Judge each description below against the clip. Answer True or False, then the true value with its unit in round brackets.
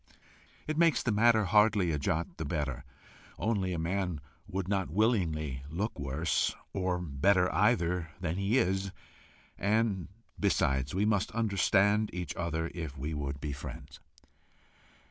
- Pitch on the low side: True (90 Hz)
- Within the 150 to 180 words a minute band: False (140 wpm)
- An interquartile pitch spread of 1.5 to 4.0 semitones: False (4.7 semitones)